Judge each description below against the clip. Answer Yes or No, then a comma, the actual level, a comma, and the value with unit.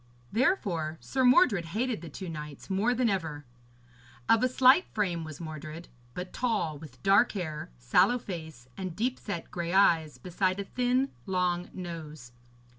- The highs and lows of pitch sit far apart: Yes, wide, 6.2 semitones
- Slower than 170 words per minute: Yes, average, 155 wpm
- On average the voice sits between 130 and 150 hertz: No, medium, 180 Hz